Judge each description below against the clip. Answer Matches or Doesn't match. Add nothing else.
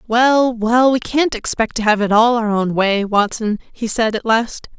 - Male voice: Doesn't match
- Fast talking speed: Matches